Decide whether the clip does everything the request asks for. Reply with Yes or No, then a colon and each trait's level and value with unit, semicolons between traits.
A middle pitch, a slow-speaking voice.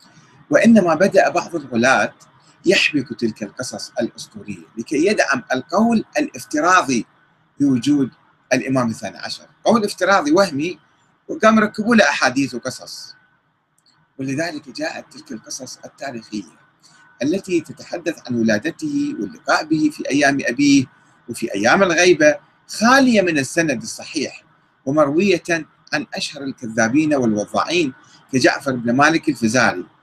No: medium, 170 Hz; average, 110 wpm